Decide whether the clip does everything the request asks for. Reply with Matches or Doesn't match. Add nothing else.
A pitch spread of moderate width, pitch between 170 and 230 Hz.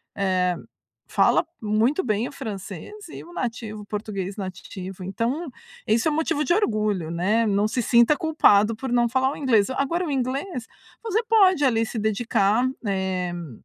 Doesn't match